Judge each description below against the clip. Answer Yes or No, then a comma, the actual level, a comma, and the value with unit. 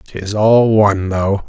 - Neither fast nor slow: Yes, average, 160 wpm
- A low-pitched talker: Yes, low, 100 Hz